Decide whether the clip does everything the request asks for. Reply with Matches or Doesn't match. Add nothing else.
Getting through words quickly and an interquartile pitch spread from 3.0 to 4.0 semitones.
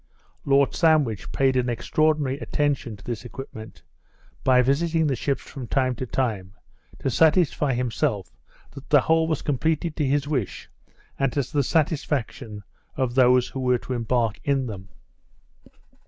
Doesn't match